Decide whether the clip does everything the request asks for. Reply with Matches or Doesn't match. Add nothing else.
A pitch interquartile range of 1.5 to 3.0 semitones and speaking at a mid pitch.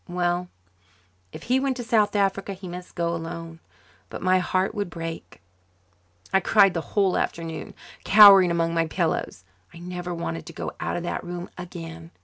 Matches